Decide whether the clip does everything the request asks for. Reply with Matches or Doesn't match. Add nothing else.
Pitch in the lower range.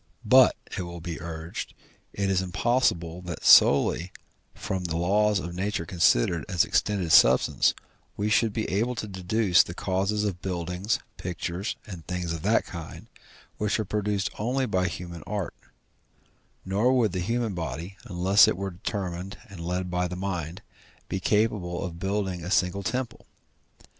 Matches